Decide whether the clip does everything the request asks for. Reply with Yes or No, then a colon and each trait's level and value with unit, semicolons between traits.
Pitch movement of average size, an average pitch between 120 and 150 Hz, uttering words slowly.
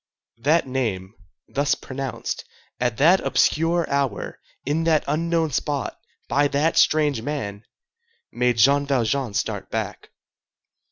Yes: average, 3.7 semitones; medium, 140 Hz; slow, 115 wpm